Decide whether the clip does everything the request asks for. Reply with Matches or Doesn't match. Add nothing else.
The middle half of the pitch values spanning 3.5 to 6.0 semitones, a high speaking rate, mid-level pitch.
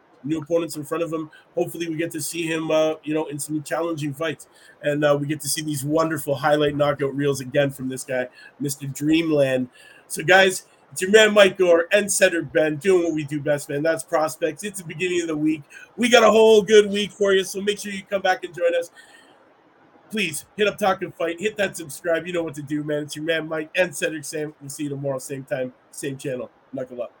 Matches